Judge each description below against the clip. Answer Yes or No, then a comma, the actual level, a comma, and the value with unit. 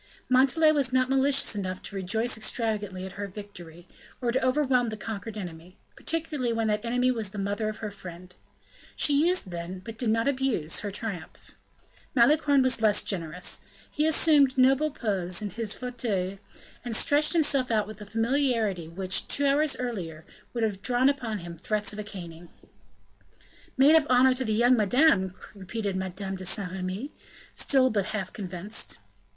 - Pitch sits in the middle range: No, high, 220 Hz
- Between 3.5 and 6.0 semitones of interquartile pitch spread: Yes, average, 5.3 semitones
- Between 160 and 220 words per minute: Yes, average, 170 wpm